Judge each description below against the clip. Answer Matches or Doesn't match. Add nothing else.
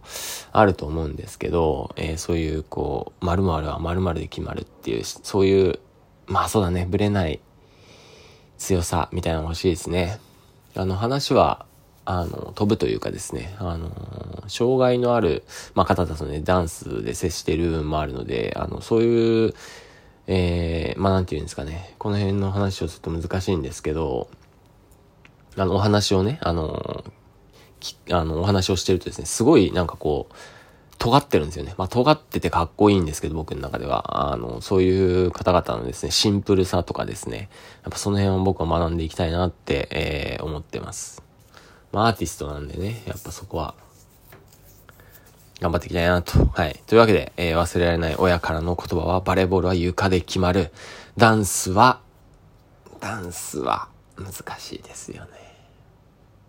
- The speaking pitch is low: Matches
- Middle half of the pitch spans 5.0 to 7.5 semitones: Doesn't match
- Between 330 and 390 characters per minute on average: Matches